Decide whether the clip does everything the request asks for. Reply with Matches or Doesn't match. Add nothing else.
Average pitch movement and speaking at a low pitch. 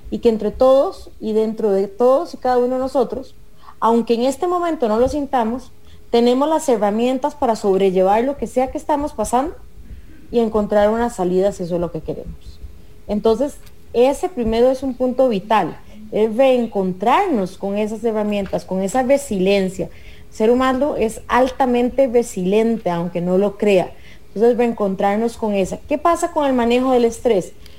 Doesn't match